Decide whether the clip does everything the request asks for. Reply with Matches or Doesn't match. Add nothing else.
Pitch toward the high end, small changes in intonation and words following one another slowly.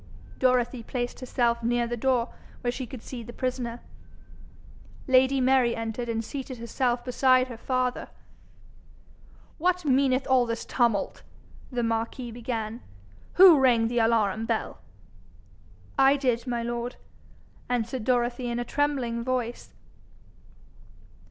Matches